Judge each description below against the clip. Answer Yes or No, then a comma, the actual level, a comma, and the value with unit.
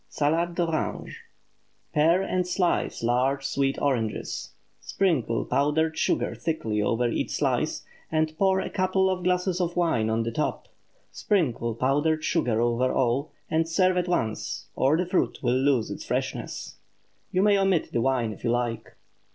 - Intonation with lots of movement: Yes, wide, 6.7 semitones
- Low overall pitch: No, medium, 150 Hz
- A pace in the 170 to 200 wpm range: No, average, 155 wpm